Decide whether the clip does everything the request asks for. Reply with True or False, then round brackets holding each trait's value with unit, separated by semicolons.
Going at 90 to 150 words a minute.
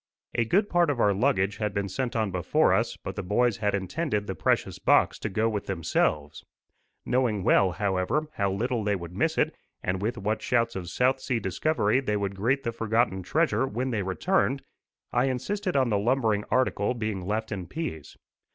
False (195 wpm)